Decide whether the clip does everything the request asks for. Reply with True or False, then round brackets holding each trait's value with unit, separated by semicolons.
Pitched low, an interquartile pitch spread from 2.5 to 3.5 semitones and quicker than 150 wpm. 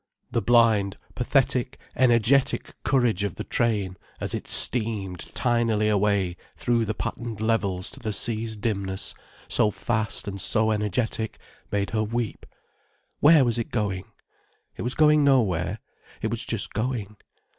False (110 Hz; 2.9 semitones; 140 wpm)